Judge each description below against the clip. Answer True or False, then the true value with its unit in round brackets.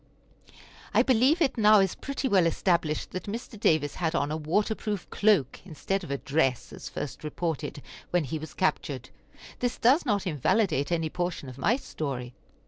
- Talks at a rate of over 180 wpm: False (175 wpm)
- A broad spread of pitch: True (6.1 semitones)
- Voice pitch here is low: False (175 Hz)